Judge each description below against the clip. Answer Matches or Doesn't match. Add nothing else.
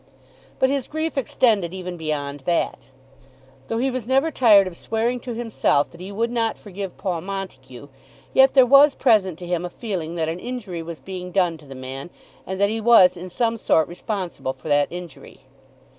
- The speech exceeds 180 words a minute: Matches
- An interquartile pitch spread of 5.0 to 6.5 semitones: Matches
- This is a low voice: Doesn't match